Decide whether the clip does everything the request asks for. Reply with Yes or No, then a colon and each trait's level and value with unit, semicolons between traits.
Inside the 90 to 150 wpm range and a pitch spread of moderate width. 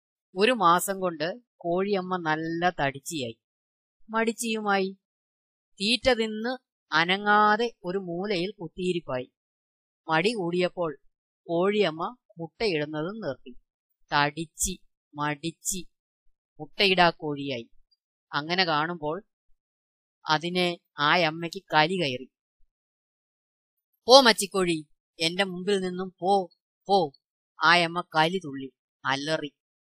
No: average, 80 wpm; average, 4.8 semitones